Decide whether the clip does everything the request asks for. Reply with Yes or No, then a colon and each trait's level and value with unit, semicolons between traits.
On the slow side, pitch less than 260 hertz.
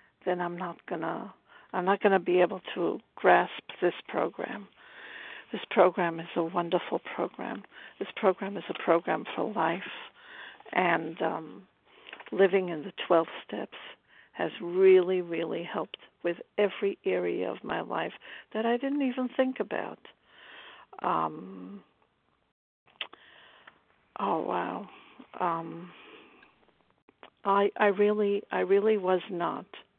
Yes: slow, 125 wpm; medium, 185 Hz